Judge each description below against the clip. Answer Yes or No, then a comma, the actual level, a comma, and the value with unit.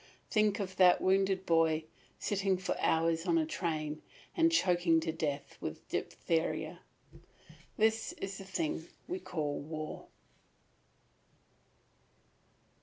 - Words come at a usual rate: No, slow, 110 wpm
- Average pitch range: Yes, average, 3.3 semitones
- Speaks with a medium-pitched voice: Yes, medium, 175 Hz